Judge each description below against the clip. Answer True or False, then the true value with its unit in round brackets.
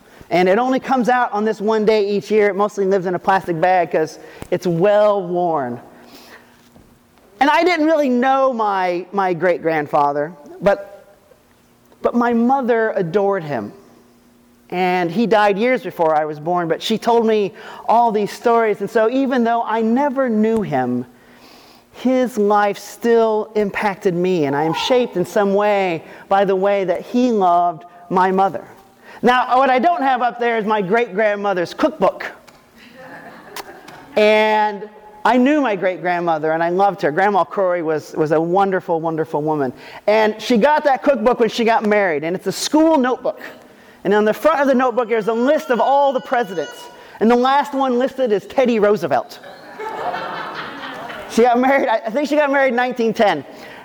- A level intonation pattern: False (5.1 semitones)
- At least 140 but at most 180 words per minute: True (175 wpm)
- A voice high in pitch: True (210 Hz)